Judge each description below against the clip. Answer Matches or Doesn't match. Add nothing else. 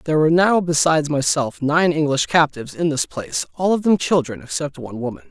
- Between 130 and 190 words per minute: Doesn't match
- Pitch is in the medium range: Matches